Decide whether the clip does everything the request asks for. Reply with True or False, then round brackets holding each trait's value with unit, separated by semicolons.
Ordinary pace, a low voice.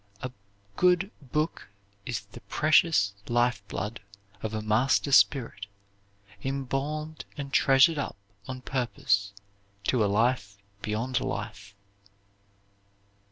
False (105 wpm; 125 Hz)